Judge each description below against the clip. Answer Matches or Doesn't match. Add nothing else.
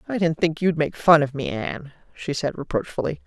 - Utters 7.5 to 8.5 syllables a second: Doesn't match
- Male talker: Doesn't match